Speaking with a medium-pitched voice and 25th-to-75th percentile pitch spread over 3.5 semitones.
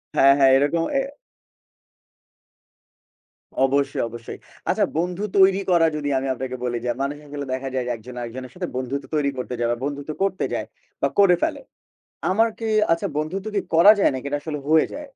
Yes: medium, 145 Hz; average, 5.3 semitones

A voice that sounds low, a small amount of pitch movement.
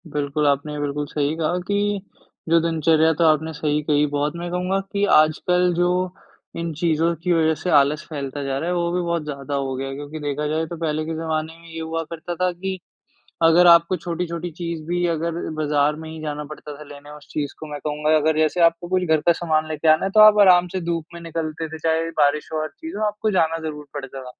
No: medium, 160 Hz; narrow, 2.3 semitones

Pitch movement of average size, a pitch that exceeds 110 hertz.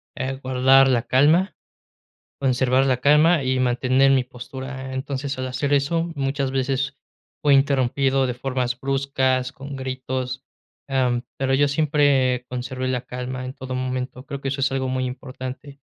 No: narrow, 1.3 semitones; low, 130 Hz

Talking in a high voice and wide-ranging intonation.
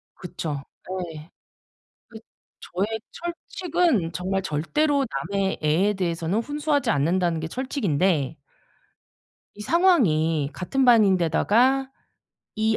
Yes: high, 195 Hz; wide, 8.3 semitones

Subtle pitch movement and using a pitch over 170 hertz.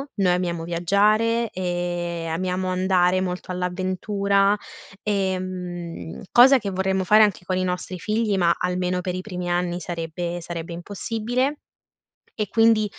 Yes: narrow, 2.3 semitones; medium, 185 Hz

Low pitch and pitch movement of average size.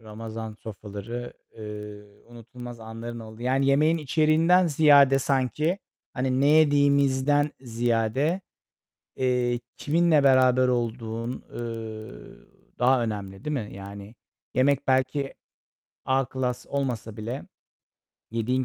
Yes: low, 125 Hz; average, 3.8 semitones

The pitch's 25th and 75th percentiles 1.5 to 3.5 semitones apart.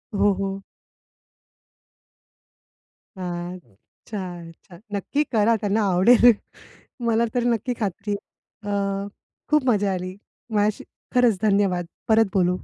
Yes: average, 3.1 semitones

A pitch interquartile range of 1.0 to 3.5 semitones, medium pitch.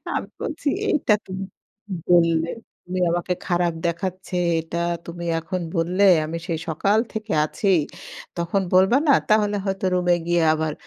Yes: narrow, 2.6 semitones; medium, 180 Hz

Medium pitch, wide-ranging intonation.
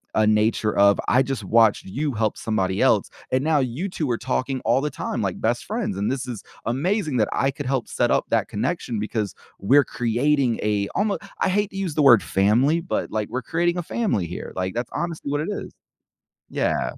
No: low, 125 Hz; wide, 5.7 semitones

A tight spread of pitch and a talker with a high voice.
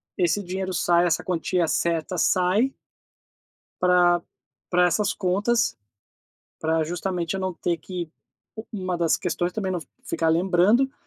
No: narrow, 1.8 semitones; medium, 180 Hz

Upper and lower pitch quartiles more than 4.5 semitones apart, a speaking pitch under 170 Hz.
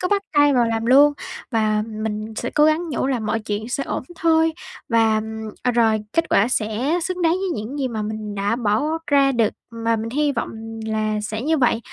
No: average, 5.0 semitones; high, 230 Hz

